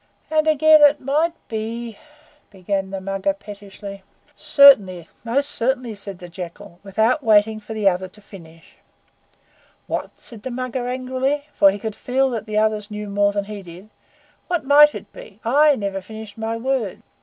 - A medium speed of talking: Yes, average, 170 wpm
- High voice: Yes, high, 220 Hz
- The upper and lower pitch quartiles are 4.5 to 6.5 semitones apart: Yes, average, 4.9 semitones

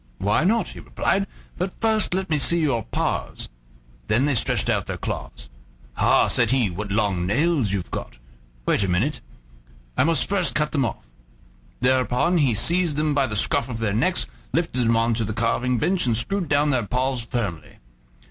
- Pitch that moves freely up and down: Yes, wide, 5.9 semitones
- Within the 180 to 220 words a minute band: Yes, average, 185 wpm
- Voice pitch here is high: No, low, 130 Hz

